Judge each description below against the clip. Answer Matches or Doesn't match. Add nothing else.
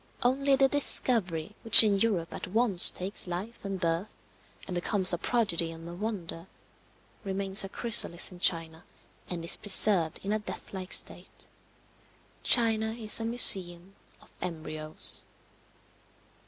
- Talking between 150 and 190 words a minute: Doesn't match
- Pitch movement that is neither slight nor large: Matches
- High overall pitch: Matches